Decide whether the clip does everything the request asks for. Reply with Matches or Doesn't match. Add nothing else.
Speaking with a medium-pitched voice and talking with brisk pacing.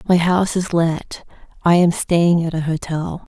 Doesn't match